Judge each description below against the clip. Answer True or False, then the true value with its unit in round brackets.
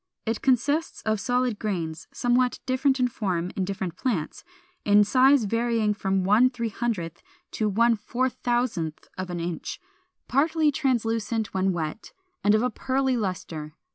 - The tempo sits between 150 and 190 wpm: False (135 wpm)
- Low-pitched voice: False (225 Hz)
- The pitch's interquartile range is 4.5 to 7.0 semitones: True (4.9 semitones)